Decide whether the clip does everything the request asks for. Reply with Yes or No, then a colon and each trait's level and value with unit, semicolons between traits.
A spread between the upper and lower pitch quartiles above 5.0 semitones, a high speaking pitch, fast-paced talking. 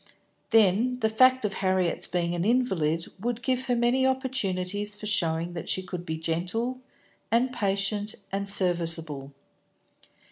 No: wide, 5.4 semitones; high, 200 Hz; average, 140 wpm